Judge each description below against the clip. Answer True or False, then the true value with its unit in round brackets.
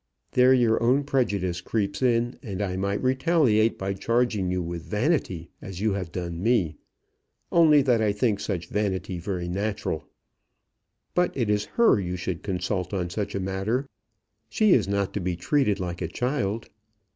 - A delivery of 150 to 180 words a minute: True (170 wpm)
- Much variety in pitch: False (4.8 semitones)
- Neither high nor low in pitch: False (100 Hz)